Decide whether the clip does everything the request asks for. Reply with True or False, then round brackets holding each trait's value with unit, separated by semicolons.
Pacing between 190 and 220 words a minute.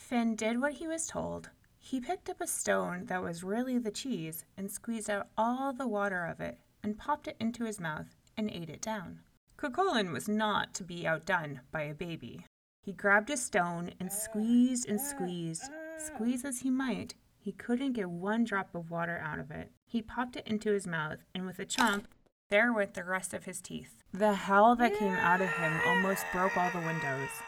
True (205 wpm)